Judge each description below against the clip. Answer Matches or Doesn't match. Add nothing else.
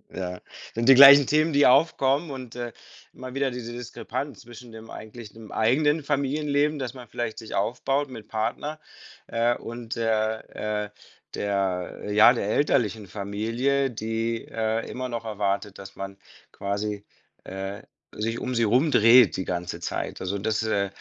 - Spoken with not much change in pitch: Doesn't match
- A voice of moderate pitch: Doesn't match